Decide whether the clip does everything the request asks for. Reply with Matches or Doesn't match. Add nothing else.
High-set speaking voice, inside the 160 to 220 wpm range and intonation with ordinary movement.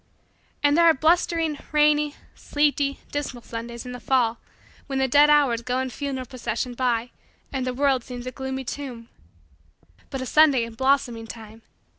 Matches